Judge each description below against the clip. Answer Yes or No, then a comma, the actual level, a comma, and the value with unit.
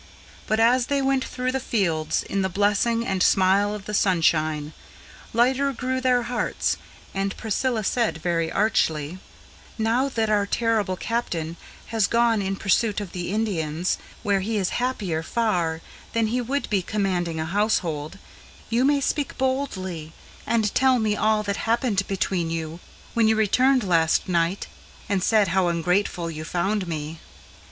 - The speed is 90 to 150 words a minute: No, average, 160 wpm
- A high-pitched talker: Yes, high, 205 Hz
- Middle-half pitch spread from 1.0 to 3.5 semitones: No, average, 5.0 semitones